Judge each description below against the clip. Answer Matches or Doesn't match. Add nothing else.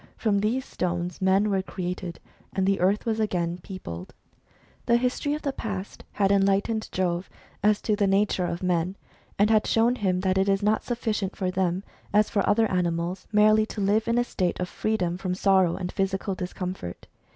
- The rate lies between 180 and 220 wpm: Matches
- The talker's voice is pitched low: Doesn't match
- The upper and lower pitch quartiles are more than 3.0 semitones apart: Doesn't match